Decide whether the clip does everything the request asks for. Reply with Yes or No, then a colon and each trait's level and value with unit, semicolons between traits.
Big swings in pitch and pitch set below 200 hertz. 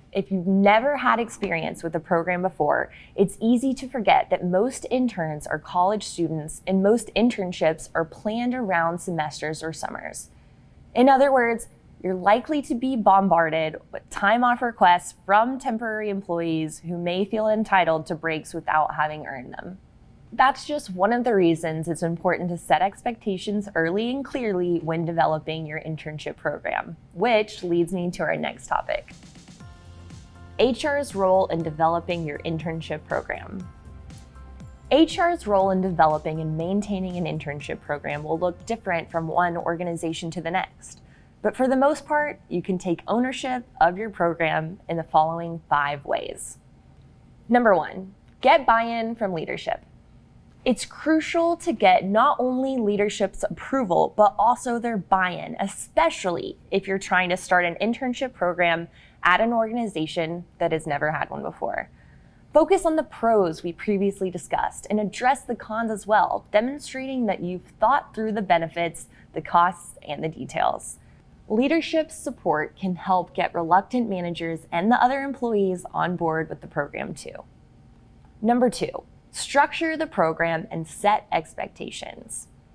Yes: wide, 5.9 semitones; medium, 185 Hz